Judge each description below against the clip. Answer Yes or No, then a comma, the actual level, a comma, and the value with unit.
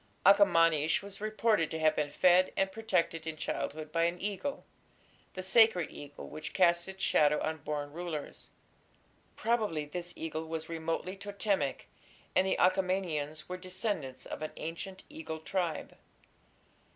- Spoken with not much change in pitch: No, average, 3.5 semitones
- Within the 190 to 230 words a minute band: No, average, 140 wpm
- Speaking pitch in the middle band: Yes, medium, 170 Hz